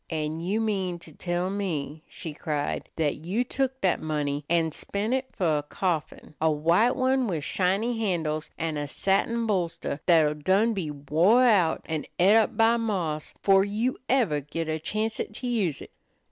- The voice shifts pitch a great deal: Yes, wide, 5.8 semitones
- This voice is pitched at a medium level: Yes, medium, 180 Hz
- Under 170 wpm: No, average, 175 wpm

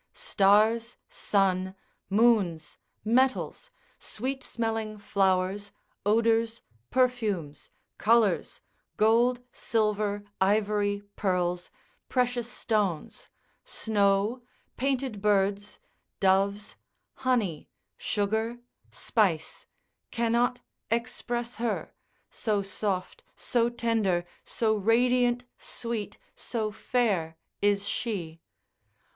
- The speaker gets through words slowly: Yes, slow, 75 wpm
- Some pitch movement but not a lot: Yes, average, 3.1 semitones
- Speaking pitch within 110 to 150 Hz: No, high, 215 Hz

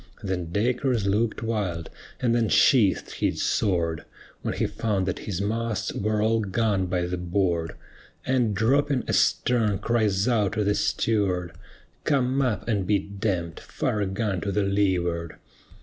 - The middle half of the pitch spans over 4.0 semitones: No, average, 3.5 semitones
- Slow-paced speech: No, average, 155 wpm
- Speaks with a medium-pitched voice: No, low, 105 Hz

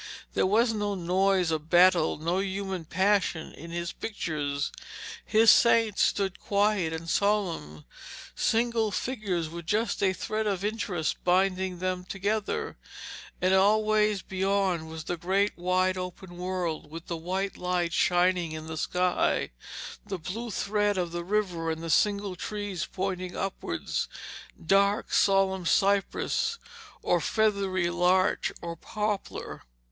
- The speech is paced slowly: Yes, slow, 130 wpm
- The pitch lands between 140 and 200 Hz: Yes, medium, 185 Hz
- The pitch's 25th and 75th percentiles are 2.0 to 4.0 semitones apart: Yes, average, 2.8 semitones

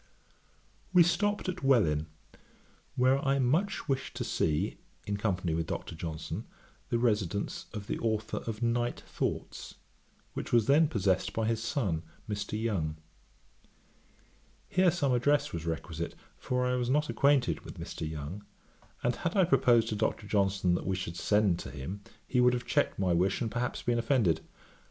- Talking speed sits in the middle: Yes, average, 165 wpm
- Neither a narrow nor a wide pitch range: No, wide, 5.8 semitones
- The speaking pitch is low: Yes, low, 110 Hz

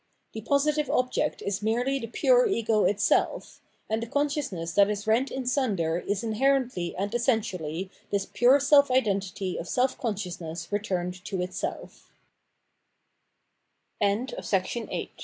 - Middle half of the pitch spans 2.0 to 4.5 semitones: No, average, 5.1 semitones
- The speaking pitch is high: Yes, high, 220 Hz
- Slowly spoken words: Yes, slow, 110 wpm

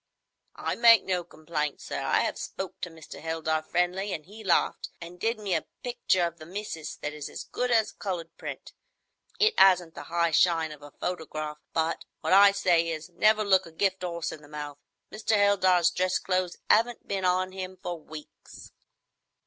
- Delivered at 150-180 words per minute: No, average, 190 wpm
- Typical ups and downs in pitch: Yes, average, 3.3 semitones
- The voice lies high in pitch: No, medium, 180 Hz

